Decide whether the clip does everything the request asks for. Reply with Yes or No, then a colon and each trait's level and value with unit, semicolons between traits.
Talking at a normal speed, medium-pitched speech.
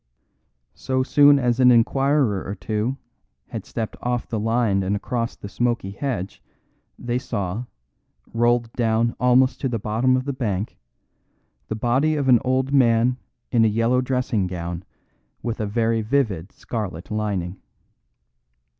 No: average, 145 wpm; low, 115 Hz